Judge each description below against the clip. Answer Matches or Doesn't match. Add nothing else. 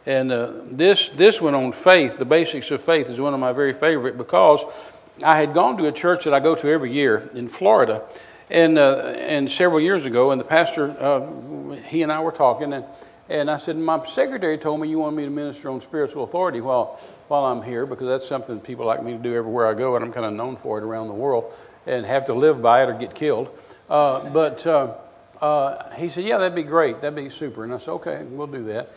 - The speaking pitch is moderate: Matches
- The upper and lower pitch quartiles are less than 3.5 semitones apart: Doesn't match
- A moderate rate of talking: Doesn't match